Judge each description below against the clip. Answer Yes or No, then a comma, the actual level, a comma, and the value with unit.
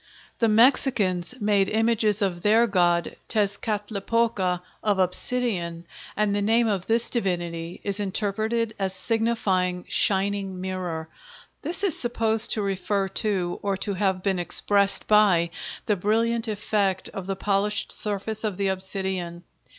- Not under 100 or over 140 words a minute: Yes, slow, 135 wpm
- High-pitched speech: Yes, high, 200 Hz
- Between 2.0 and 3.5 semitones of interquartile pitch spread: Yes, average, 2.8 semitones